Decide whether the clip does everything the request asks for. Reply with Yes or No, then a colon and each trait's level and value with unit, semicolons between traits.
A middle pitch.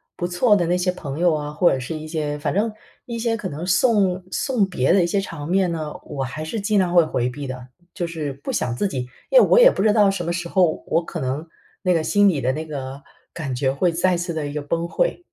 Yes: medium, 170 Hz